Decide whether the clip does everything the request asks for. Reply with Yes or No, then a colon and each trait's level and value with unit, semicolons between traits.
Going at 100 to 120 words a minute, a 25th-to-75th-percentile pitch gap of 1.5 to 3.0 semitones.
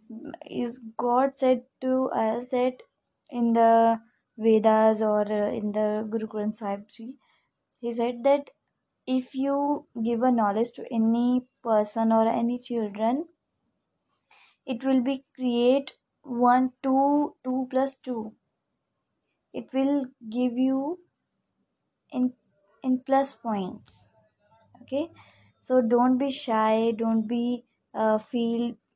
Yes: average, 115 wpm; average, 2.7 semitones